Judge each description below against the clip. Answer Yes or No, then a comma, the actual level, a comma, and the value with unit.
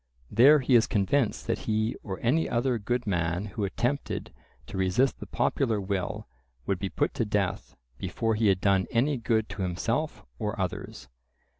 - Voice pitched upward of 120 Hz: No, low, 110 Hz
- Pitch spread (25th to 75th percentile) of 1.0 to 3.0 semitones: No, average, 3.9 semitones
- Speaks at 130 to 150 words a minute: No, average, 170 wpm